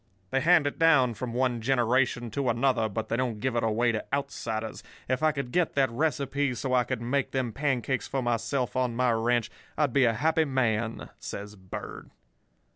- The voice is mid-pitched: No, low, 125 Hz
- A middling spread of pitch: Yes, average, 3.0 semitones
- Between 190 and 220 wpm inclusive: Yes, average, 195 wpm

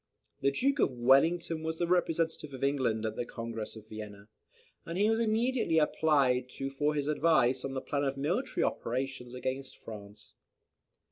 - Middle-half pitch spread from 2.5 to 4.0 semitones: No, average, 4.9 semitones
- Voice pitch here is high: No, low, 135 Hz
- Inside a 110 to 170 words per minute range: Yes, average, 165 wpm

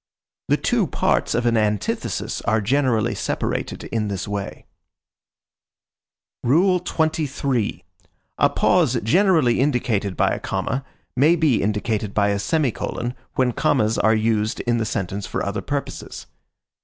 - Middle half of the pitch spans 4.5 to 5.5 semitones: Yes, average, 4.9 semitones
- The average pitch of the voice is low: Yes, low, 115 Hz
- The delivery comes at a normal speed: No, slow, 130 wpm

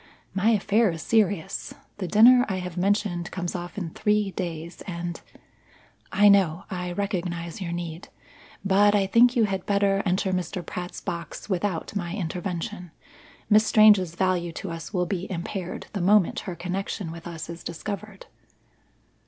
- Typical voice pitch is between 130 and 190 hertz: Yes, medium, 185 Hz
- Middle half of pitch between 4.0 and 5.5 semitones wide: No, average, 2.8 semitones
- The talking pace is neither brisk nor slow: Yes, average, 160 wpm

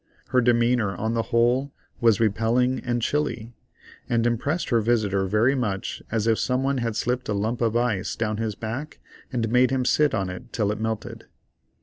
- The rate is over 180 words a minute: Yes, average, 190 wpm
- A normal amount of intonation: No, narrow, 2.3 semitones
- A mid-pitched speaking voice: No, low, 115 Hz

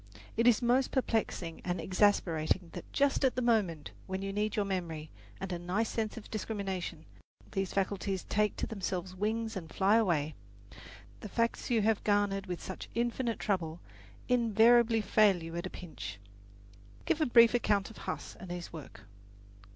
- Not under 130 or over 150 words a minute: No, average, 165 wpm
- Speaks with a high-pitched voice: Yes, high, 200 Hz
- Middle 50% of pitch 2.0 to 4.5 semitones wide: Yes, average, 3.9 semitones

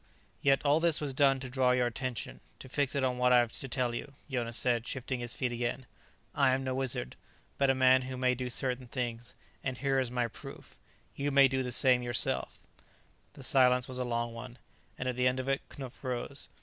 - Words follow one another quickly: Yes, fast, 225 wpm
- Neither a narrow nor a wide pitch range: No, narrow, 1.6 semitones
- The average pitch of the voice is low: Yes, low, 130 Hz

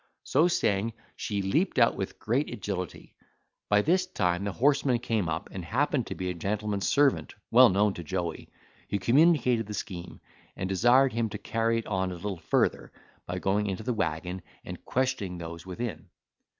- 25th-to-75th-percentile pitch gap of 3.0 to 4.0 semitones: No, average, 4.7 semitones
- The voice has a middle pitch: No, low, 105 Hz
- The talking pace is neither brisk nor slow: Yes, average, 175 wpm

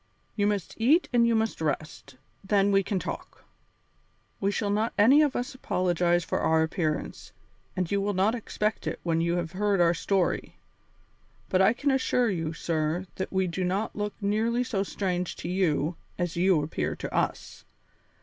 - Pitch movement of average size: Yes, average, 3.7 semitones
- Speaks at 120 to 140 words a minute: No, average, 180 wpm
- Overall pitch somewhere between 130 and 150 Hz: No, high, 190 Hz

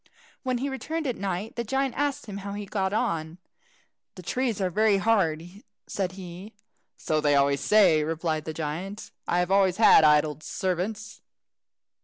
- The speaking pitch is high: Yes, high, 195 Hz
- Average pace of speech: Yes, average, 165 wpm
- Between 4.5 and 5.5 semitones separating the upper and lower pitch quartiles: Yes, average, 5.0 semitones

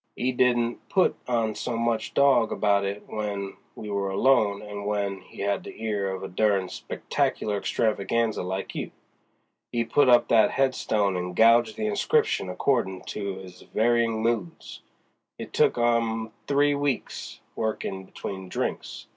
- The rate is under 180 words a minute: Yes, average, 150 wpm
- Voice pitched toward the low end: Yes, low, 110 Hz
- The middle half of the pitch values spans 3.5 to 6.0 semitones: No, average, 3.0 semitones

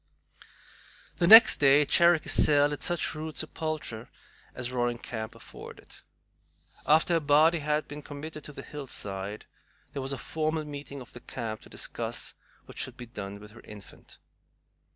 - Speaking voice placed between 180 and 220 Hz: No, medium, 145 Hz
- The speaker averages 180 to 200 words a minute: No, average, 155 wpm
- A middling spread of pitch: Yes, average, 4.4 semitones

